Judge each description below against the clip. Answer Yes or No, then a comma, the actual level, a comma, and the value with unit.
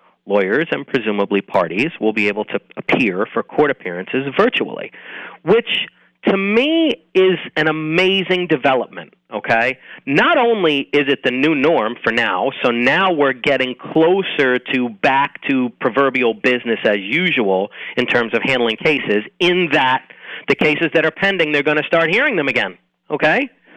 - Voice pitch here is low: No, medium, 145 Hz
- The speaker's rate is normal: Yes, average, 155 wpm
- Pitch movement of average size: No, wide, 6.5 semitones